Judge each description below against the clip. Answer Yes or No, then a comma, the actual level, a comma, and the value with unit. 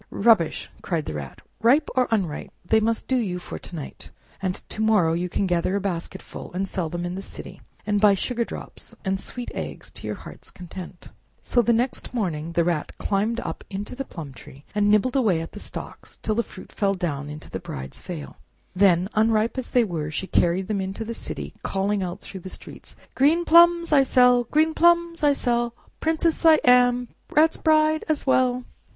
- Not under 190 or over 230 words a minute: Yes, average, 200 wpm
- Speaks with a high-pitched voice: Yes, high, 210 Hz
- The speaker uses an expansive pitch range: Yes, wide, 5.9 semitones